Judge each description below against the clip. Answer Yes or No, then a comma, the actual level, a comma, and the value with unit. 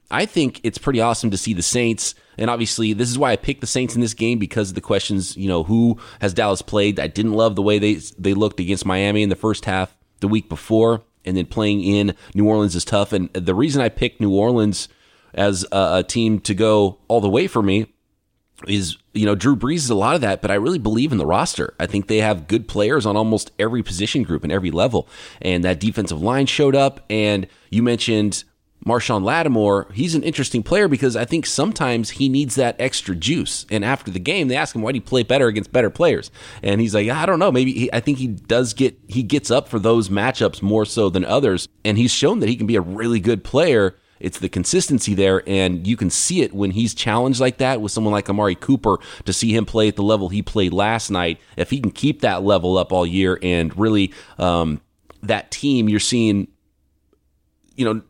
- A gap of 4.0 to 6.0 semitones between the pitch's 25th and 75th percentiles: No, average, 3.2 semitones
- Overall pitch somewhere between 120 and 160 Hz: No, low, 105 Hz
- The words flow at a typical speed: No, fast, 235 wpm